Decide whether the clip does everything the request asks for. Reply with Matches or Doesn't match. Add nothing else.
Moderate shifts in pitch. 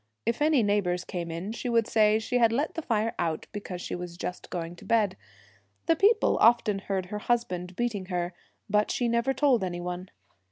Matches